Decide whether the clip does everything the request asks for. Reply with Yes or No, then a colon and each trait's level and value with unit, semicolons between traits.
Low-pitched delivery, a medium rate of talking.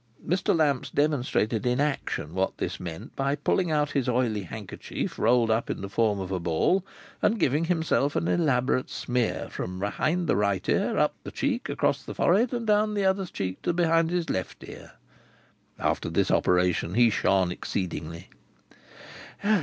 Yes: low, 125 Hz; average, 170 wpm